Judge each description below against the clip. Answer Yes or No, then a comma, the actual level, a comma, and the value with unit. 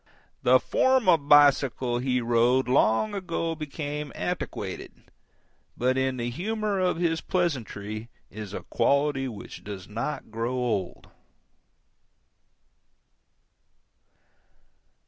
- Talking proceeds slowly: Yes, slow, 100 wpm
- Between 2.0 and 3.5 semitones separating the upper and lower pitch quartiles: No, wide, 5.6 semitones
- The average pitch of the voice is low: Yes, low, 130 Hz